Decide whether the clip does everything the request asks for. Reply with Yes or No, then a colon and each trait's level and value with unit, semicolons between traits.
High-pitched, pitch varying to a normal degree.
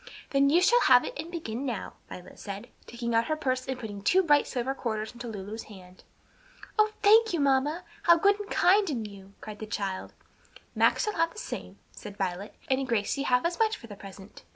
No: very high, 255 Hz; wide, 8.0 semitones